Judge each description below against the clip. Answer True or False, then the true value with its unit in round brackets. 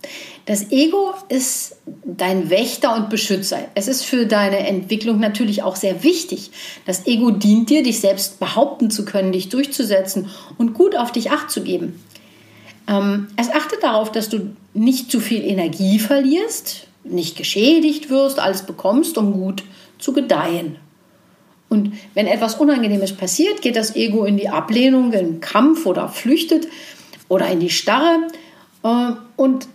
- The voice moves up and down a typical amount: False (6.4 semitones)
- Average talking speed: True (150 wpm)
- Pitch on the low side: False (225 Hz)